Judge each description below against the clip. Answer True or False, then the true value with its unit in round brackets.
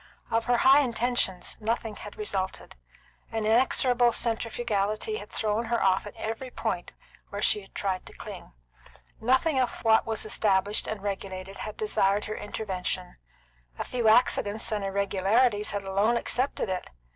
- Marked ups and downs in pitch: False (3.1 semitones)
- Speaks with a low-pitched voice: False (215 Hz)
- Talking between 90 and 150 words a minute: True (145 wpm)